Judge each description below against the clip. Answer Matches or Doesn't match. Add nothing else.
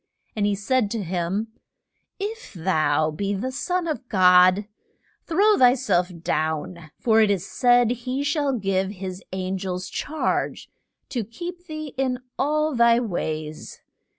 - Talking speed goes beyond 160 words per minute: Doesn't match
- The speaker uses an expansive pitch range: Matches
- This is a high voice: Matches